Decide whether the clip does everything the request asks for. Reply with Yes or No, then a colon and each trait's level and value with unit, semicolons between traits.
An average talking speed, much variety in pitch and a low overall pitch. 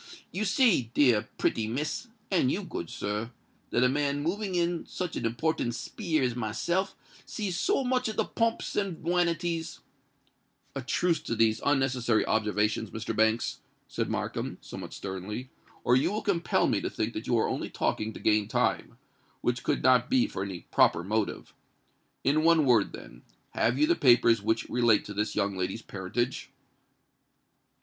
Yes: average, 160 wpm; wide, 7.6 semitones; low, 125 Hz